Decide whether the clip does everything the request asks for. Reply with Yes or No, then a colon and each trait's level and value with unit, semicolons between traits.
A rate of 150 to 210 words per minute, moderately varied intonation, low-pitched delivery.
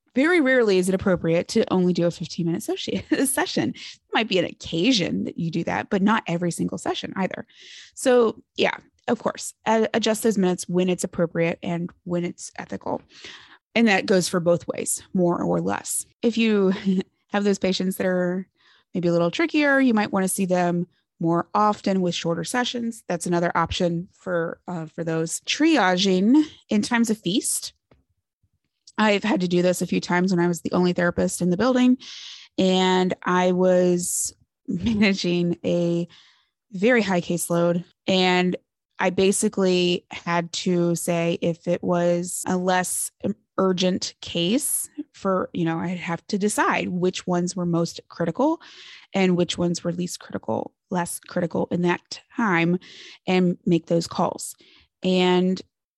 No: average, 160 wpm; average, 3.2 semitones; medium, 180 Hz